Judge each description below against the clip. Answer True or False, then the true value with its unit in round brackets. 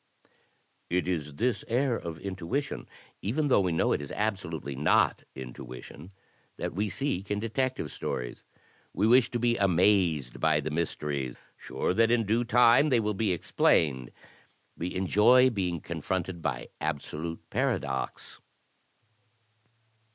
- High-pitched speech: False (95 Hz)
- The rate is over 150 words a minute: False (135 wpm)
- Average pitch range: False (6.6 semitones)